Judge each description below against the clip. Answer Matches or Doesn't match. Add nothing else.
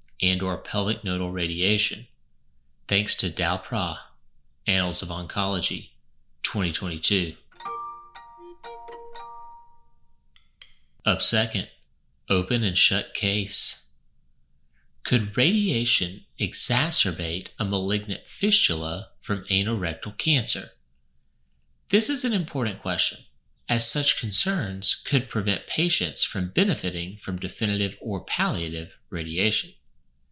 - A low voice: Matches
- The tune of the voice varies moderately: Doesn't match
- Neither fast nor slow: Doesn't match